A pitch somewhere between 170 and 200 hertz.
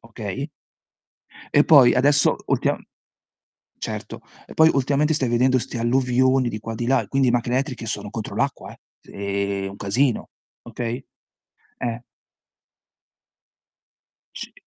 No: low, 120 Hz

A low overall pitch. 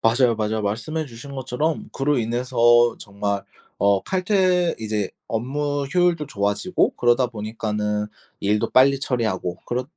Yes: low, 120 Hz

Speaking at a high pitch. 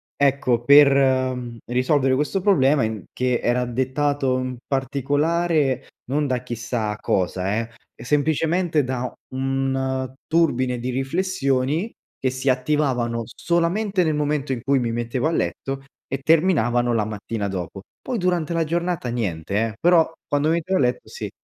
No: low, 135 Hz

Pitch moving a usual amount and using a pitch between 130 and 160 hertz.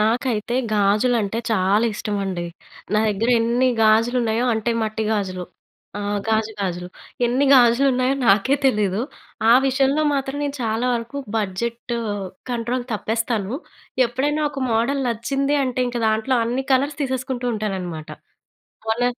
No: average, 3.2 semitones; high, 235 Hz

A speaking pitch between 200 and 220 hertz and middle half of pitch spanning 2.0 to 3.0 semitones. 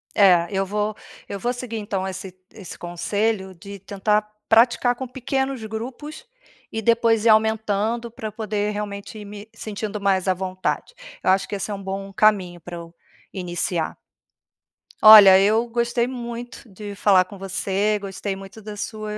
Yes: high, 210 Hz; narrow, 2.6 semitones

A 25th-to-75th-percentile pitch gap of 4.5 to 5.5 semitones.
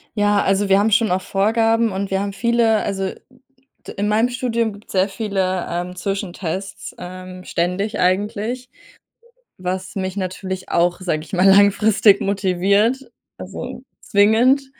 No: average, 2.9 semitones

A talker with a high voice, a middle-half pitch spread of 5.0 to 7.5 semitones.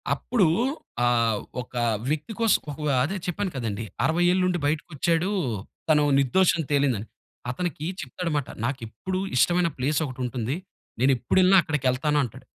No: medium, 150 Hz; wide, 5.6 semitones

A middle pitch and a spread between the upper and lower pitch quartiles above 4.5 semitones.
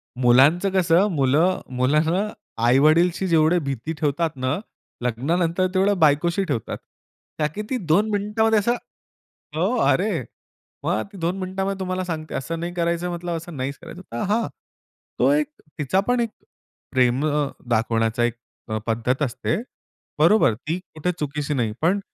Yes: medium, 165 Hz; wide, 5.5 semitones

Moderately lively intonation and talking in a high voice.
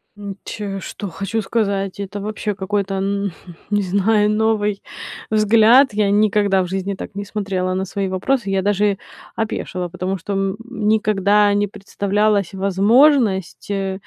No: narrow, 1.5 semitones; high, 200 Hz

